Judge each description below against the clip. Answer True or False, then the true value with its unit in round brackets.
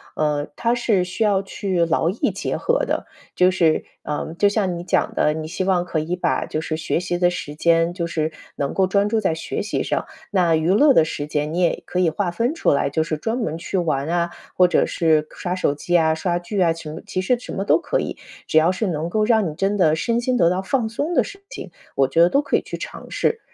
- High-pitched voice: False (175 Hz)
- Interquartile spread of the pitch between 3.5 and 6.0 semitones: True (4.0 semitones)